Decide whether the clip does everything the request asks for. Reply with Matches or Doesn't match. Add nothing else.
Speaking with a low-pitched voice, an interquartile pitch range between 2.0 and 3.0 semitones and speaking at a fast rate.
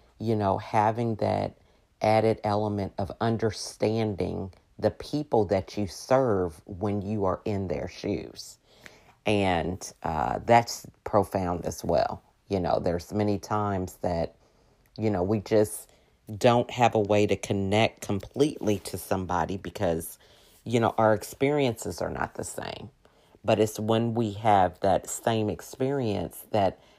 Doesn't match